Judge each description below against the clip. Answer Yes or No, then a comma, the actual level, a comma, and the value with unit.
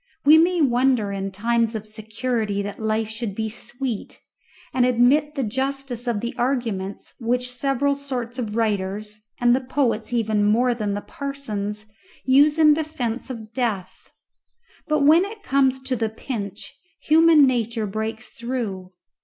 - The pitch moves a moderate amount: Yes, average, 3.9 semitones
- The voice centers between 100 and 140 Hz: No, high, 240 Hz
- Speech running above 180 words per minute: No, average, 150 wpm